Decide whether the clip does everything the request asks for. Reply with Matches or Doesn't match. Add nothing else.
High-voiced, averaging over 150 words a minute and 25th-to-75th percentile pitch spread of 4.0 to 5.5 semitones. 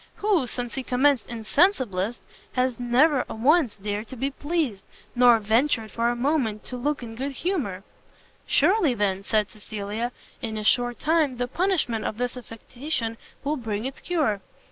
Matches